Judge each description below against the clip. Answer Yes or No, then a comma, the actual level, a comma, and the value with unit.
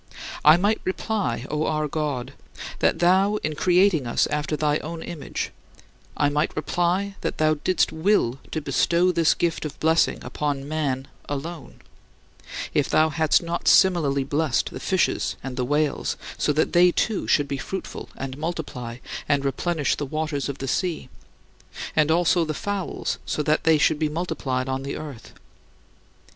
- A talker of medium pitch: Yes, medium, 155 Hz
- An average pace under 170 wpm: Yes, average, 160 wpm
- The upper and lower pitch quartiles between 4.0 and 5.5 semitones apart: No, average, 3.3 semitones